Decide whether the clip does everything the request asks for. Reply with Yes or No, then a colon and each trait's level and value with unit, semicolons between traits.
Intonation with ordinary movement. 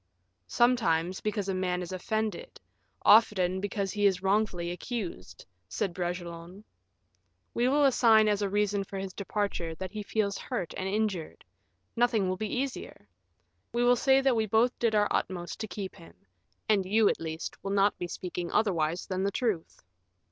Yes: average, 3.4 semitones